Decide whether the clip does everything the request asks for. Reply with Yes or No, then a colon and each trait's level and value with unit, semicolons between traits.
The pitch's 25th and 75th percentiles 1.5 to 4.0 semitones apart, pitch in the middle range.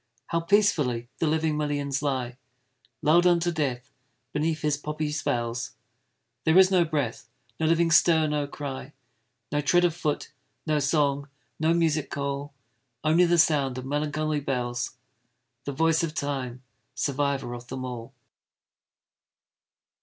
Yes: average, 3.0 semitones; medium, 150 Hz